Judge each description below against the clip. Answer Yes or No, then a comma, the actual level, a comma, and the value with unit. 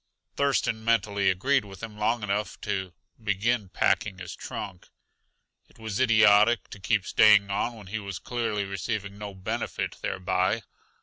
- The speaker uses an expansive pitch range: No, narrow, 2.4 semitones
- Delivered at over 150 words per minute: No, average, 145 wpm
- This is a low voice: Yes, low, 105 Hz